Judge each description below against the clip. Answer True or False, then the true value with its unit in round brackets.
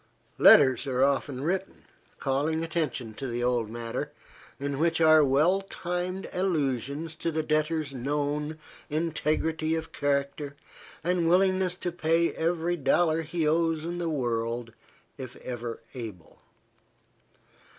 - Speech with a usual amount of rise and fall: True (3.8 semitones)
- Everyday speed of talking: False (125 wpm)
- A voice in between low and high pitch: True (155 Hz)